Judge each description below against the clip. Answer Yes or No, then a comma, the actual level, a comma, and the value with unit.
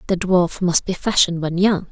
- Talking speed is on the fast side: Yes, fast, 220 wpm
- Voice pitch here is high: No, medium, 180 Hz